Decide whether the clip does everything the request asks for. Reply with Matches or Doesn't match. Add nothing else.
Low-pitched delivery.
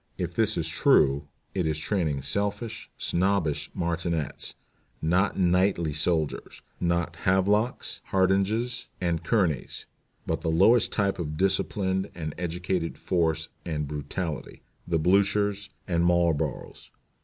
Matches